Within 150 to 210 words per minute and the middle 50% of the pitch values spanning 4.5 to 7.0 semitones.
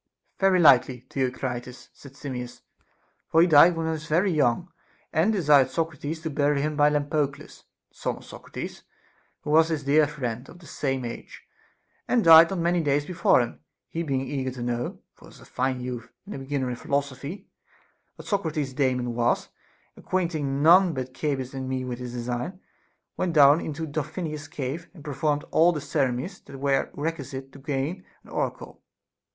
No: average, 180 wpm; average, 3.7 semitones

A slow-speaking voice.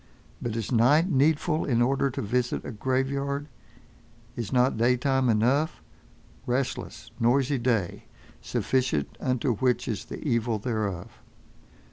Yes: slow, 115 wpm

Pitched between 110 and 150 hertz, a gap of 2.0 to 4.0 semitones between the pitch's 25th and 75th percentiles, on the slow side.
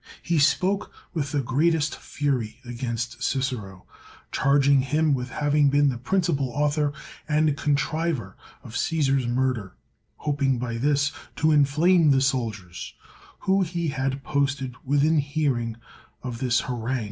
Yes: medium, 140 Hz; average, 3.0 semitones; slow, 130 wpm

